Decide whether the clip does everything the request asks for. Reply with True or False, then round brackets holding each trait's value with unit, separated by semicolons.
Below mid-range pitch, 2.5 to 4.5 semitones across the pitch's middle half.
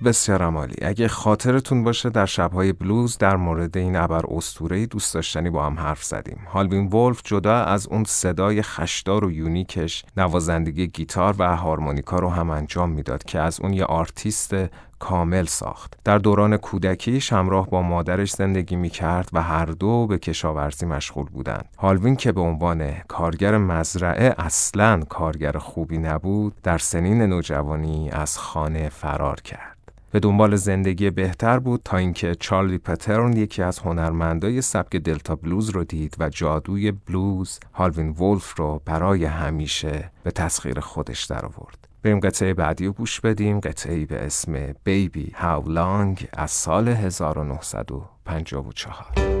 True (90 Hz; 4.0 semitones)